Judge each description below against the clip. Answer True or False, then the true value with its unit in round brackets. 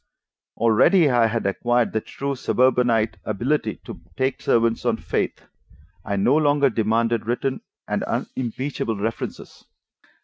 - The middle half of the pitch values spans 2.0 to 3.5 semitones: True (2.8 semitones)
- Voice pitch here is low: True (120 Hz)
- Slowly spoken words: True (125 wpm)